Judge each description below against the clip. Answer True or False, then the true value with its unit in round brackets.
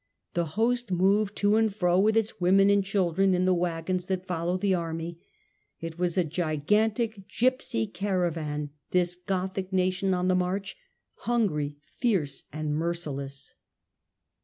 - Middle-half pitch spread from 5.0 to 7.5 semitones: False (3.1 semitones)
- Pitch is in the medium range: True (180 Hz)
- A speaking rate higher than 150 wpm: False (145 wpm)